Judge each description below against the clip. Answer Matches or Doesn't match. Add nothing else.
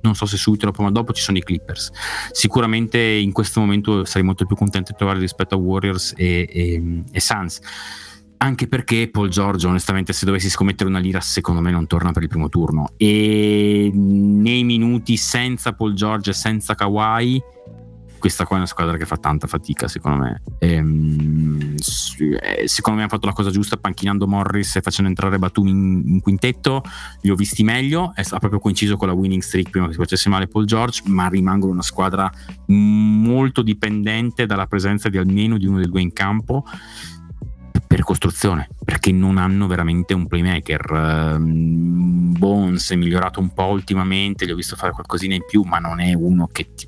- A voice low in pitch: Matches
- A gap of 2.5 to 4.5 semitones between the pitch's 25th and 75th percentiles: Matches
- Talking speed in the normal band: Doesn't match